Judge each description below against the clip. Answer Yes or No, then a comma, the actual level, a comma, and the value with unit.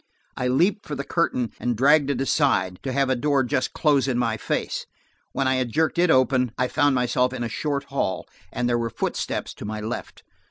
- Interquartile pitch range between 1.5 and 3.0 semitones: Yes, average, 2.7 semitones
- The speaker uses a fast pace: Yes, fast, 215 wpm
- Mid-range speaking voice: No, low, 130 Hz